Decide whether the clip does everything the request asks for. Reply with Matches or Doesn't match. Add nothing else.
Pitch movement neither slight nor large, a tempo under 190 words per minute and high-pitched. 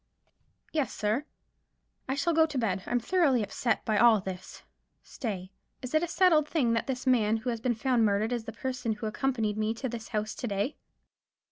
Doesn't match